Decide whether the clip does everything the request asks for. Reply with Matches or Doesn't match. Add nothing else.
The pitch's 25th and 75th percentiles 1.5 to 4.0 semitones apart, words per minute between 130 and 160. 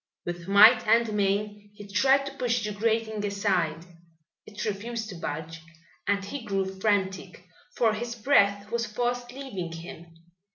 Matches